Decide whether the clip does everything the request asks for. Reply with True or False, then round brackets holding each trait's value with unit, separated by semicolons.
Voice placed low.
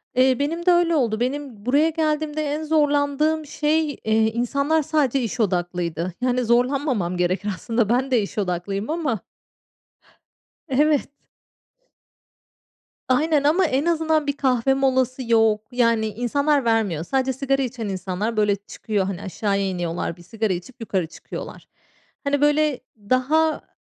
False (255 Hz)